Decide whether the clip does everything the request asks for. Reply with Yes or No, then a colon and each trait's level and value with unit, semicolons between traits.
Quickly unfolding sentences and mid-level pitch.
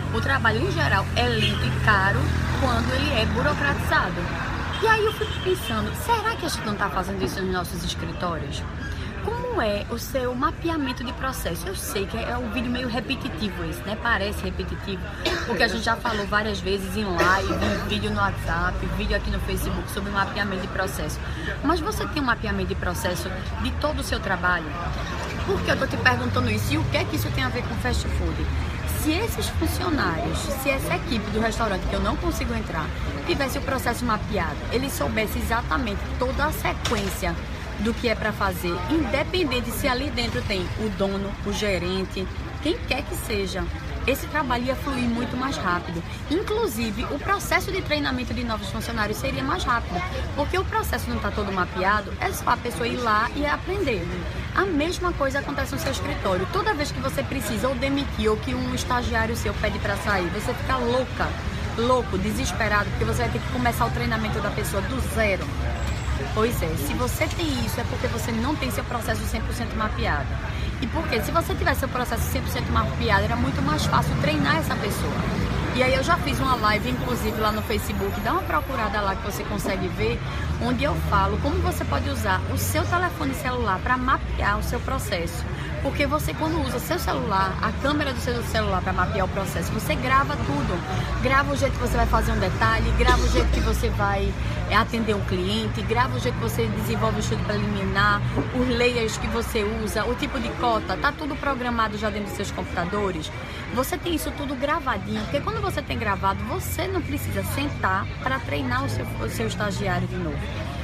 No: fast, 200 wpm; low, 120 Hz